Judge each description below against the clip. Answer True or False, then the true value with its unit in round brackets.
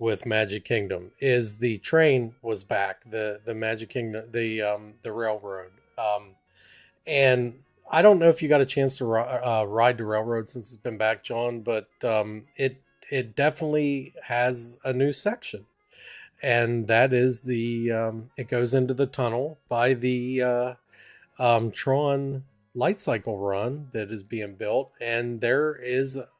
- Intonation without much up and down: False (3.0 semitones)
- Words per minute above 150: True (160 wpm)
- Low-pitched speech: True (120 Hz)